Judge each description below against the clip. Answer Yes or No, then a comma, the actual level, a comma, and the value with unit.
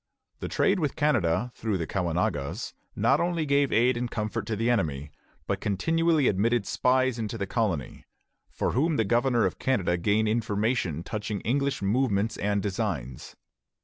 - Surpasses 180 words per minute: No, average, 155 wpm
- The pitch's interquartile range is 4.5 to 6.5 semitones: Yes, average, 4.8 semitones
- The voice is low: Yes, low, 110 Hz